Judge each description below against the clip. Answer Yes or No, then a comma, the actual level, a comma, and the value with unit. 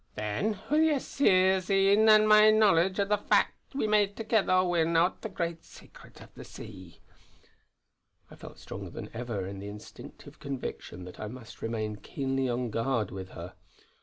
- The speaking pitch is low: No, medium, 165 Hz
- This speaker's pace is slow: No, average, 165 wpm